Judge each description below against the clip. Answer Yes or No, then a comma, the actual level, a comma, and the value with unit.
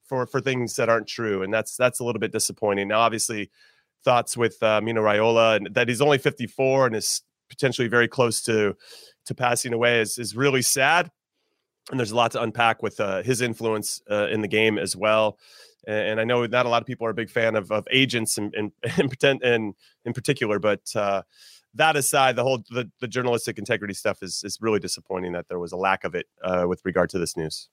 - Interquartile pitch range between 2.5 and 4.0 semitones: Yes, average, 2.8 semitones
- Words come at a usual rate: No, fast, 225 wpm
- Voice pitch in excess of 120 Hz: No, low, 115 Hz